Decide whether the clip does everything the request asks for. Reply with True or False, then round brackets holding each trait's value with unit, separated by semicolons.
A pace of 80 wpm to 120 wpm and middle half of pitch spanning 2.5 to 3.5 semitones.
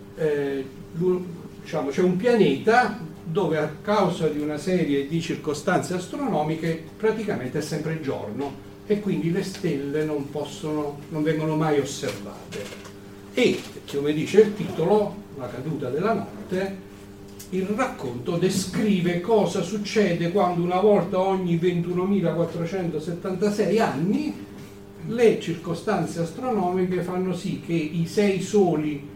False (115 wpm; 4.3 semitones)